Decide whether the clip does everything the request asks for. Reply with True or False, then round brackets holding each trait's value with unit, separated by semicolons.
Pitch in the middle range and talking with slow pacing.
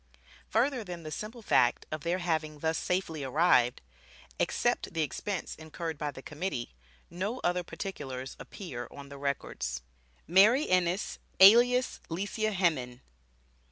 True (170 Hz; 130 wpm)